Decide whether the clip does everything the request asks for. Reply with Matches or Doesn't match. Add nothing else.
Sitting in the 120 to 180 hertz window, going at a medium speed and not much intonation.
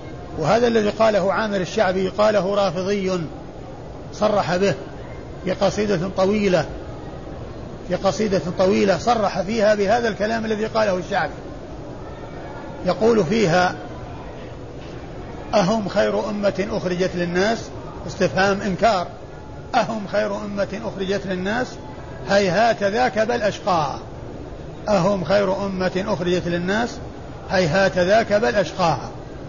Doesn't match